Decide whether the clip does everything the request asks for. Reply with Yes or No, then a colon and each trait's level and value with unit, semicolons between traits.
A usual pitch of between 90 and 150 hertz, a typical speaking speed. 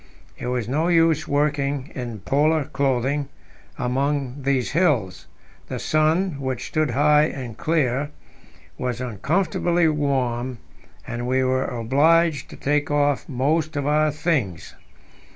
No: medium, 140 Hz; slow, 125 wpm